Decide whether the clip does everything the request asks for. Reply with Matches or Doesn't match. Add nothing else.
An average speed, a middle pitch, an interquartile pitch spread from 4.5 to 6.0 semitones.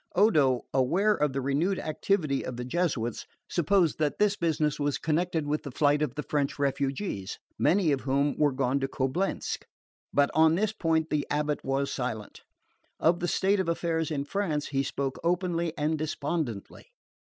Doesn't match